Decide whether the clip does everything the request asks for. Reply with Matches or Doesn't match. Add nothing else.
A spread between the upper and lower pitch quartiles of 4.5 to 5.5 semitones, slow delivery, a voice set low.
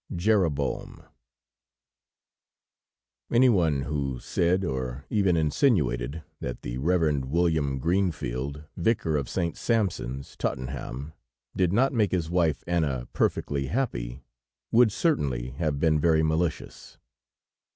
Matches